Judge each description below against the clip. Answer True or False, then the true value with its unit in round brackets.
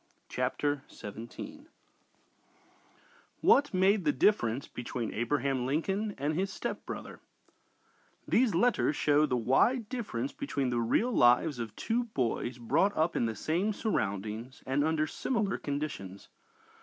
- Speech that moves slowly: True (125 wpm)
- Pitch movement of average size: False (9.0 semitones)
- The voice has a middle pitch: True (150 Hz)